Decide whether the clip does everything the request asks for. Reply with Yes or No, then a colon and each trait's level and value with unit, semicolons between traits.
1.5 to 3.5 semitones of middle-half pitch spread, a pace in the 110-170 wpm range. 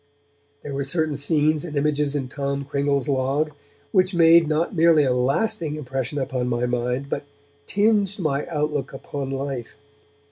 Yes: average, 2.7 semitones; average, 150 wpm